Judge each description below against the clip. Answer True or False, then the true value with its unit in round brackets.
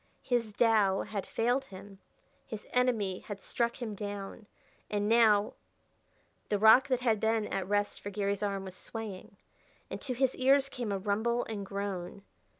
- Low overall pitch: False (210 Hz)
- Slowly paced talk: False (160 wpm)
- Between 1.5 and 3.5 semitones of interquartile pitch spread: True (2.9 semitones)